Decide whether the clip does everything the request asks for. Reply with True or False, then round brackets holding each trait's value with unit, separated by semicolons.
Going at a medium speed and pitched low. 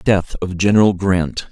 True (160 wpm; 95 Hz)